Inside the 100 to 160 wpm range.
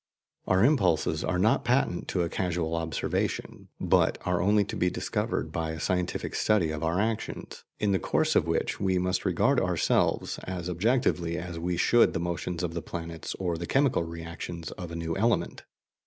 No: average, 185 wpm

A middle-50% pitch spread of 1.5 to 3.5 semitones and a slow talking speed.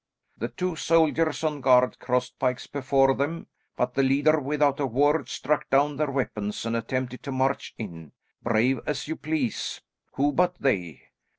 No: average, 2.8 semitones; average, 165 wpm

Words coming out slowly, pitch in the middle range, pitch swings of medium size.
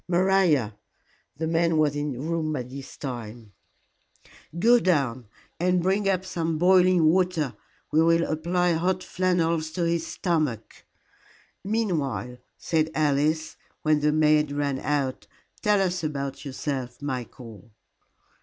Yes: slow, 125 wpm; medium, 155 Hz; average, 4.2 semitones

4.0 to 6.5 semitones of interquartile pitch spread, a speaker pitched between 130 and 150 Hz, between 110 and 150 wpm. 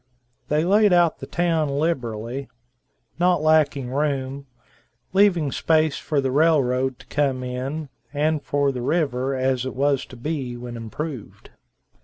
No: average, 3.5 semitones; medium, 140 Hz; average, 140 wpm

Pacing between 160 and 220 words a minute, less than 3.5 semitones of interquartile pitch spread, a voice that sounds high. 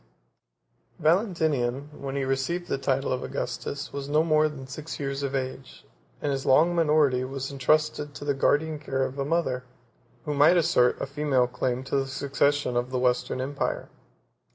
No: average, 175 wpm; narrow, 2.4 semitones; medium, 140 Hz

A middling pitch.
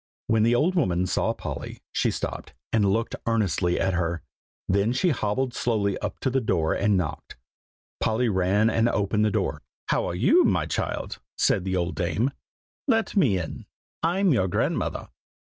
No: low, 105 Hz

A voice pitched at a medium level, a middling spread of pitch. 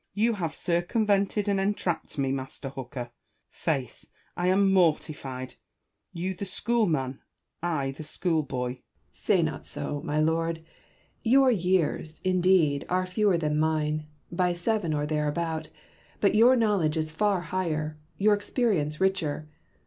Yes: medium, 170 Hz; average, 4.2 semitones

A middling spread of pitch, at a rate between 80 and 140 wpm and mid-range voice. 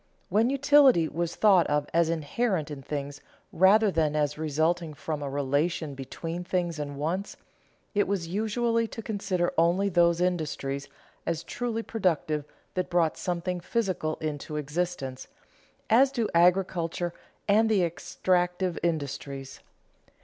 Yes: average, 4.2 semitones; slow, 135 wpm; medium, 170 Hz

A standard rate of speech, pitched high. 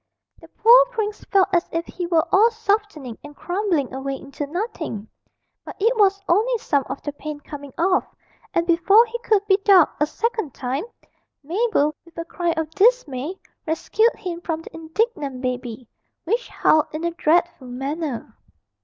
Yes: average, 165 wpm; very high, 340 Hz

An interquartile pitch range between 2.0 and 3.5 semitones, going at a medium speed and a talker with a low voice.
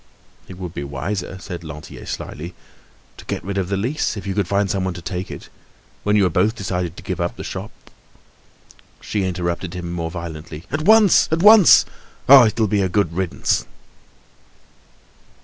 Yes: average, 3.1 semitones; average, 180 wpm; very low, 95 Hz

